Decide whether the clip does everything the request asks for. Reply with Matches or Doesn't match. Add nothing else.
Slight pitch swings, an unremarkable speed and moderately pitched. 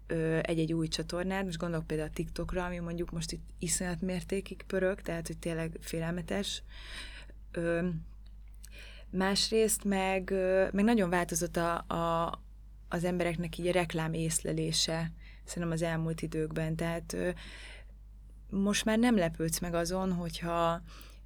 Matches